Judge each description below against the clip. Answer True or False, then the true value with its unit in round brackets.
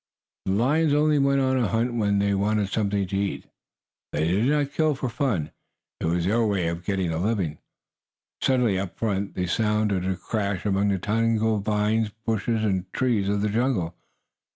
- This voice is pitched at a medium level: False (105 Hz)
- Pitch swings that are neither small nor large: True (3.3 semitones)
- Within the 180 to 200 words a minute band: True (185 wpm)